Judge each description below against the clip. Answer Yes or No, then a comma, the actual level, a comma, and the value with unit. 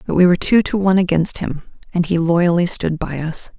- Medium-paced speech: No, fast, 235 wpm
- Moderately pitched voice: Yes, medium, 175 Hz